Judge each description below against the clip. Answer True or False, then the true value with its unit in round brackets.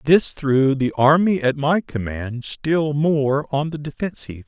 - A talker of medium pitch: True (145 Hz)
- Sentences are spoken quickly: False (160 wpm)